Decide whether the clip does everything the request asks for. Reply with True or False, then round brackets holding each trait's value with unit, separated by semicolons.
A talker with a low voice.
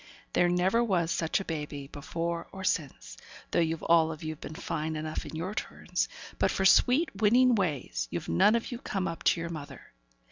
False (170 Hz)